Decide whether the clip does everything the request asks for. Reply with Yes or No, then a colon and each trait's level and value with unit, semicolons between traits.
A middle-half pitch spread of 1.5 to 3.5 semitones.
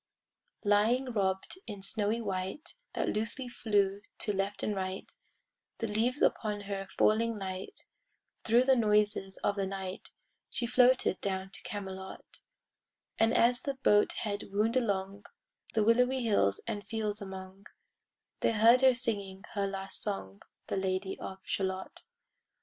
Yes: average, 3.0 semitones